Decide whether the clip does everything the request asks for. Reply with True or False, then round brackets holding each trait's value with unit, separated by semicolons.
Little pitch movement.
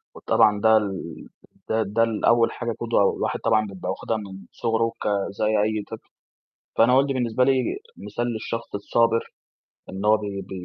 True (2.0 semitones)